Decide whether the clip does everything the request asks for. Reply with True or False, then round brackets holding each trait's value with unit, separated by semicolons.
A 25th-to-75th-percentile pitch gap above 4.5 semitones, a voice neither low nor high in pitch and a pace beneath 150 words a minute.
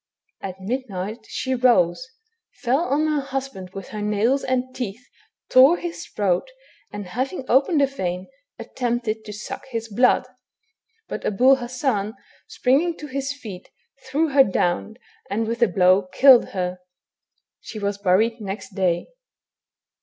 False (5.1 semitones; 235 Hz; 140 wpm)